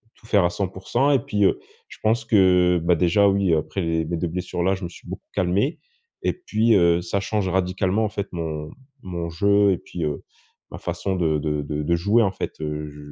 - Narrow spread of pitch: No, average, 3.1 semitones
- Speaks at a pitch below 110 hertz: Yes, very low, 90 Hz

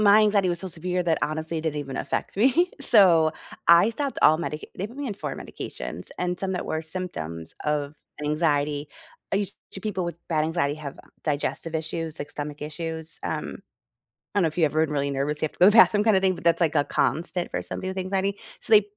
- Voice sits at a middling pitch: Yes, medium, 165 Hz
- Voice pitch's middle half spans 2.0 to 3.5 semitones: No, average, 4.0 semitones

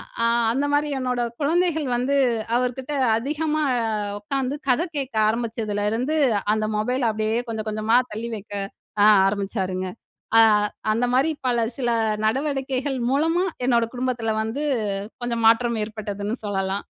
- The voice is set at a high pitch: Yes, high, 240 Hz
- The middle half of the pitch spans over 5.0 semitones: No, average, 4.0 semitones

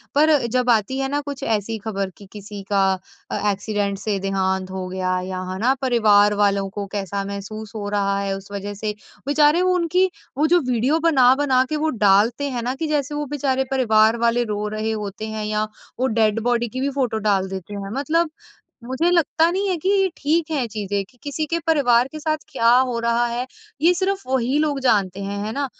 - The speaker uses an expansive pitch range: Yes, wide, 6.0 semitones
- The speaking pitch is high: Yes, high, 235 Hz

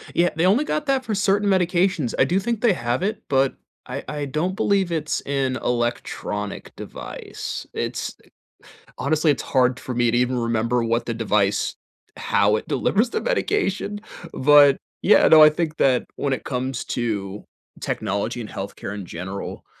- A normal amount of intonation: No, wide, 7.8 semitones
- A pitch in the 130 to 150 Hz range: Yes, low, 135 Hz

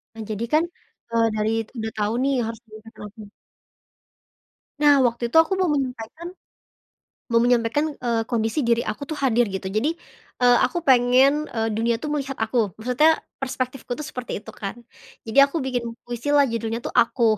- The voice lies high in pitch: Yes, high, 240 Hz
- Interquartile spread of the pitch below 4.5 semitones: Yes, average, 3.3 semitones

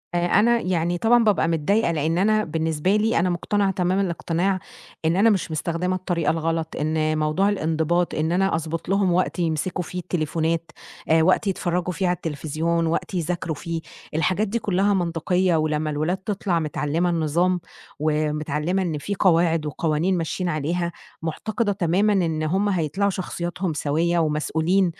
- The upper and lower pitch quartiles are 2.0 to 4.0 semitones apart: Yes, average, 2.8 semitones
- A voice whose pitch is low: No, medium, 170 Hz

